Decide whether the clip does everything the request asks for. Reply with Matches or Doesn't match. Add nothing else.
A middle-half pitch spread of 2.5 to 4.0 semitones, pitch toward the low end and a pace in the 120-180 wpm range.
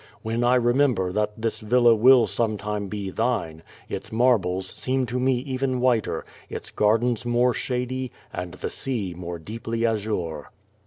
Matches